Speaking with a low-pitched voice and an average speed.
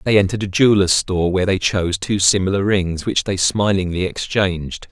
Yes: very low, 95 Hz; average, 185 wpm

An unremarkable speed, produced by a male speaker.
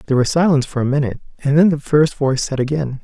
No: fast, 255 wpm; male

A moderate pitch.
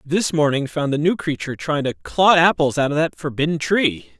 Yes: medium, 155 Hz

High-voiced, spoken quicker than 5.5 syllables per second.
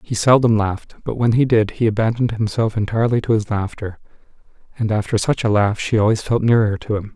No: low, 110 Hz; 6.2 syllables/s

